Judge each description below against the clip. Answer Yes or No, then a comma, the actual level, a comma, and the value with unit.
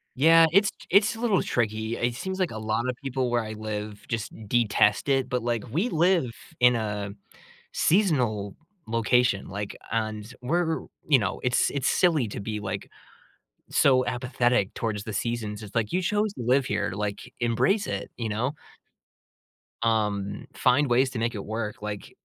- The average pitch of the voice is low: Yes, low, 120 Hz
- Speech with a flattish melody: No, average, 4.2 semitones